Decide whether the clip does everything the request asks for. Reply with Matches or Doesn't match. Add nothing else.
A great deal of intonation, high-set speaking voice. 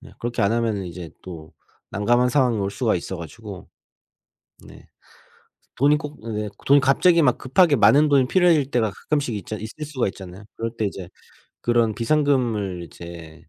Doesn't match